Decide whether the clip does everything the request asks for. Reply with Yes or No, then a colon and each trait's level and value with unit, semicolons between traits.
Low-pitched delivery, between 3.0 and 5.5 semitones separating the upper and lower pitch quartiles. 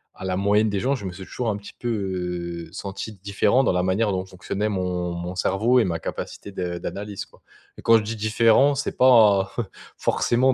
Yes: low, 100 Hz; average, 3.4 semitones